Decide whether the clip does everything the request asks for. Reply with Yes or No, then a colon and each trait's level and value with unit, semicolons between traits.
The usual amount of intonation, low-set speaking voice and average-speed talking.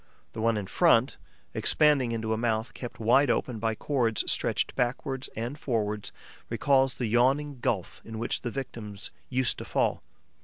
Yes: average, 3.1 semitones; low, 120 Hz; average, 160 wpm